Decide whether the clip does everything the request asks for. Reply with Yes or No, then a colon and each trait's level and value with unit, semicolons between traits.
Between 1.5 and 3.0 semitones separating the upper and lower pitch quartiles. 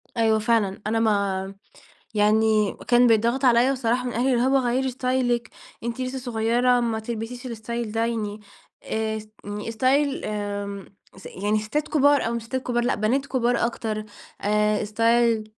Yes: narrow, 2.5 semitones